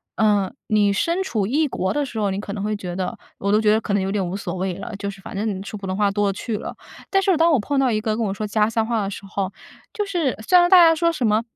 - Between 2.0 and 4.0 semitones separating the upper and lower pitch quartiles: No, average, 4.5 semitones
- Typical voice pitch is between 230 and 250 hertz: No, high, 210 Hz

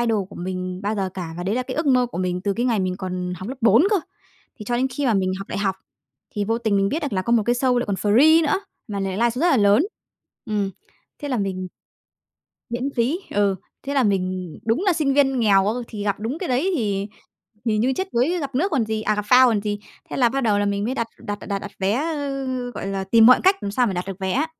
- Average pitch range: Yes, average, 4.8 semitones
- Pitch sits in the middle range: No, high, 220 Hz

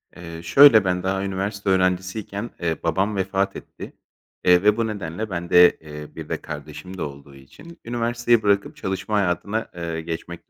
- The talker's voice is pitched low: Yes, very low, 95 Hz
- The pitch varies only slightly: No, average, 3.6 semitones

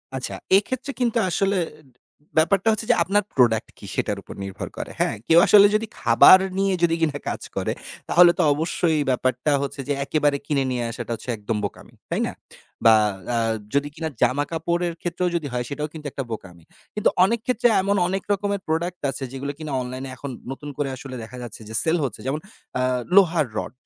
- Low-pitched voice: No, medium, 155 Hz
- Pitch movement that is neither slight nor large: No, wide, 6.4 semitones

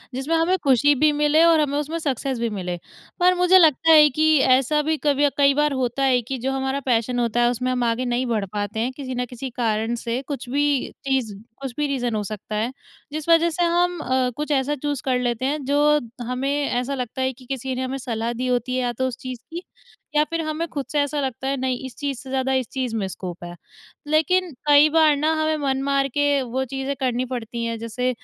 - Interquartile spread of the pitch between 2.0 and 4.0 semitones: Yes, average, 3.2 semitones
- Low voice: No, very high, 265 Hz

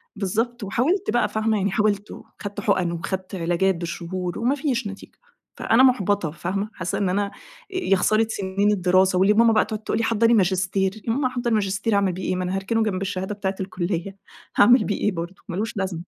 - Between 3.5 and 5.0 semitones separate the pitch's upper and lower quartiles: No, average, 2.9 semitones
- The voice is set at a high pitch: Yes, high, 200 Hz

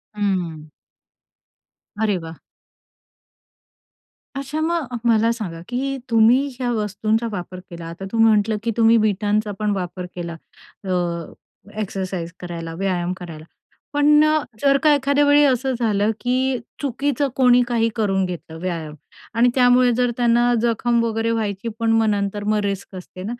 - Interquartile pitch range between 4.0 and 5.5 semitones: Yes, average, 4.4 semitones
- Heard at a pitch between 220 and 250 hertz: Yes, high, 225 Hz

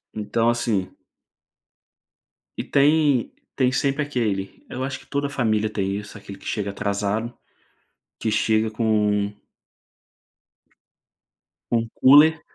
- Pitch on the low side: Yes, low, 110 Hz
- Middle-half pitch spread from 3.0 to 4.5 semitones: Yes, average, 4.2 semitones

